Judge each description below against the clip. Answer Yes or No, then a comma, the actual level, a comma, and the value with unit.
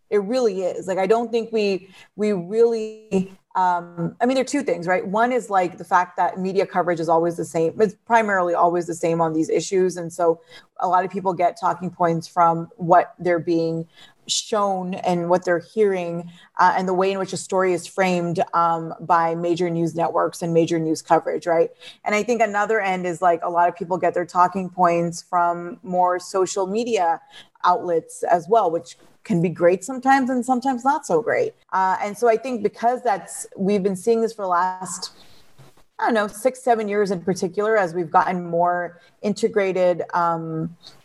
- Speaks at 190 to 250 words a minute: Yes, average, 200 wpm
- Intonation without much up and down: No, average, 3.3 semitones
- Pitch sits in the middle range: Yes, medium, 180 Hz